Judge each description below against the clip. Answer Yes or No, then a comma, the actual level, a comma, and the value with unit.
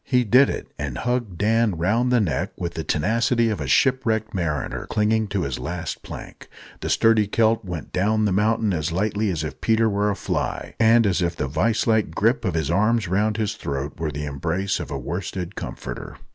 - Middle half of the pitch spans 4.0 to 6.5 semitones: Yes, average, 5.0 semitones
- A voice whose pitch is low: Yes, low, 105 Hz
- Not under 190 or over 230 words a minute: Yes, fast, 205 wpm